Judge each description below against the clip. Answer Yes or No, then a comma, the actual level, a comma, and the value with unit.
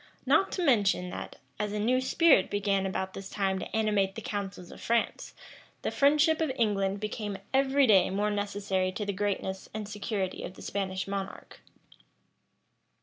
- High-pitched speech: Yes, high, 205 Hz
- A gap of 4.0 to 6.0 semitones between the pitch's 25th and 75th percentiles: No, average, 2.9 semitones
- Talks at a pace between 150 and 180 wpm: Yes, average, 165 wpm